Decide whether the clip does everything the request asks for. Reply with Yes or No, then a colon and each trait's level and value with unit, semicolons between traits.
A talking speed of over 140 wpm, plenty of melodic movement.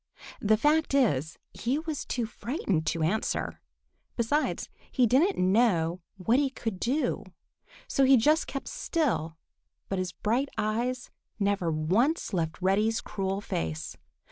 No: slow, 135 wpm; wide, 6.5 semitones